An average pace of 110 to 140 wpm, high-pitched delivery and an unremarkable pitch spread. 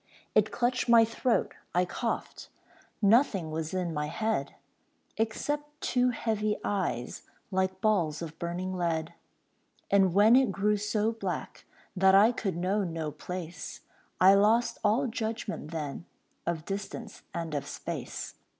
Yes: slow, 135 wpm; high, 195 Hz; average, 4.6 semitones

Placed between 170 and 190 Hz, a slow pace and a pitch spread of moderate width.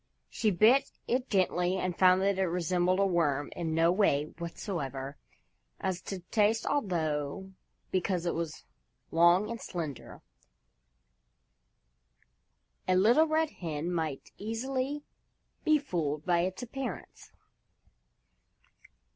Yes: medium, 185 Hz; slow, 115 wpm; average, 4.5 semitones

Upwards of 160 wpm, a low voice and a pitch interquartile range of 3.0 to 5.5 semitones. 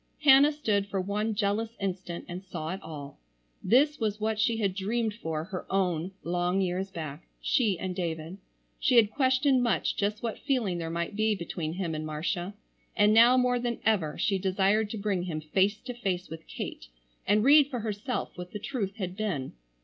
No: average, 190 wpm; high, 200 Hz; average, 4.0 semitones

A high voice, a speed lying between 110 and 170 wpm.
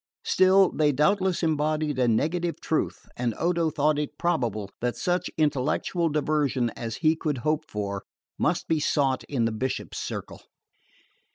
No: medium, 150 Hz; average, 150 wpm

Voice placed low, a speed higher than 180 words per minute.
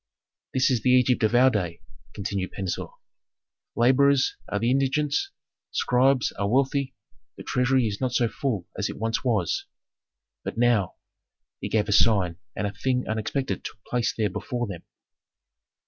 No: low, 120 Hz; average, 160 wpm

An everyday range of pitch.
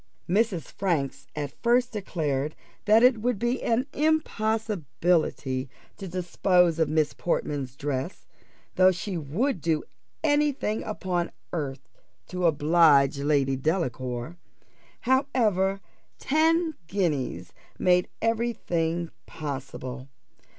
No: wide, 7.1 semitones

